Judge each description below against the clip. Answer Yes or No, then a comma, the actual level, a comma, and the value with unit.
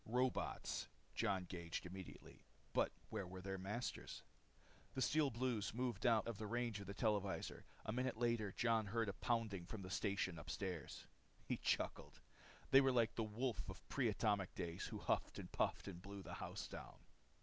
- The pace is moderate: Yes, average, 175 wpm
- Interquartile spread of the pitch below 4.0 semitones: Yes, average, 3.6 semitones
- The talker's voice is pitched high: No, low, 105 Hz